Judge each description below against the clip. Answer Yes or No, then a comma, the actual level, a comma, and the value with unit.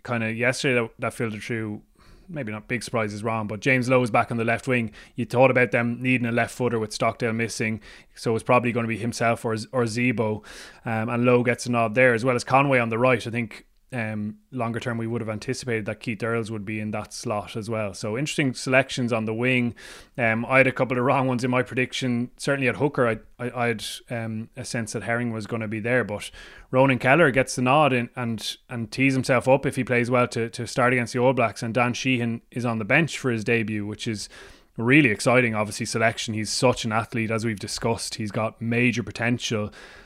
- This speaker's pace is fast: Yes, fast, 240 wpm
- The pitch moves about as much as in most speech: No, narrow, 2.0 semitones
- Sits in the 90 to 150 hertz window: Yes, low, 120 Hz